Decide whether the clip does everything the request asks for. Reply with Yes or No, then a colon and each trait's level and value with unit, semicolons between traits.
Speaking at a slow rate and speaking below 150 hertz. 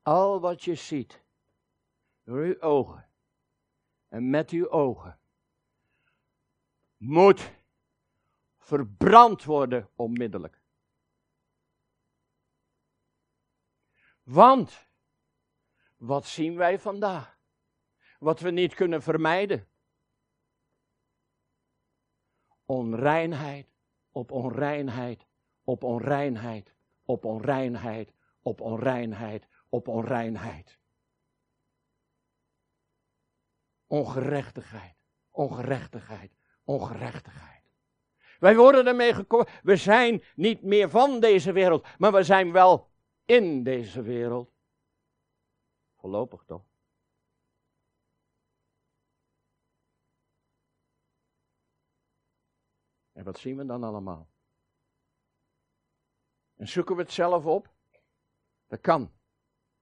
Yes: slow, 75 wpm; medium, 140 Hz